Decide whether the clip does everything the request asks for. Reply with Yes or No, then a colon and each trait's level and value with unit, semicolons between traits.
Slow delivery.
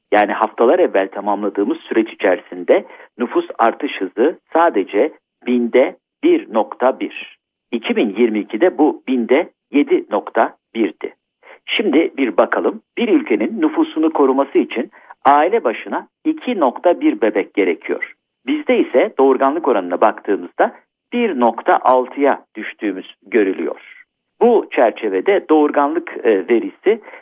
Yes: slow, 90 wpm